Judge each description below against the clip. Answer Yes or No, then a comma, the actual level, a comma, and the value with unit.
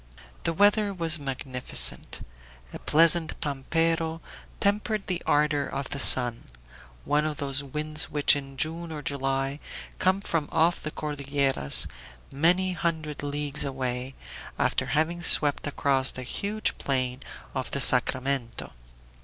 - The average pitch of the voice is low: No, medium, 145 Hz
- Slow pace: Yes, slow, 130 wpm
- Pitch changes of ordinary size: Yes, average, 3.4 semitones